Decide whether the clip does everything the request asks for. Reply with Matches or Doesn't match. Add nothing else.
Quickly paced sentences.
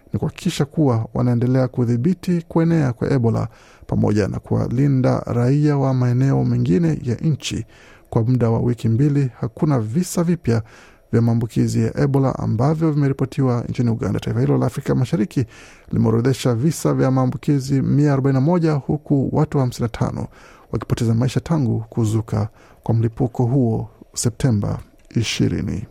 Doesn't match